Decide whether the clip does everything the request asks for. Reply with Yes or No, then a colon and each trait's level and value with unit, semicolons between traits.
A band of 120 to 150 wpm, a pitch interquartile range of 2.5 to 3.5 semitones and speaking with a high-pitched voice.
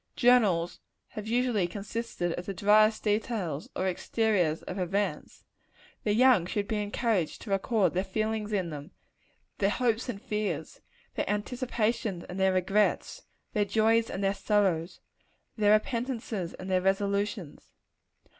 Yes: slow, 135 wpm; average, 3.0 semitones; high, 205 Hz